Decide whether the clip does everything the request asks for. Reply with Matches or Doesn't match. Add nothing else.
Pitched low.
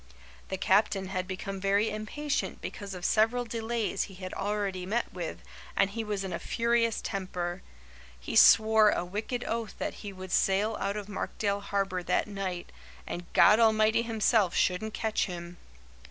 Doesn't match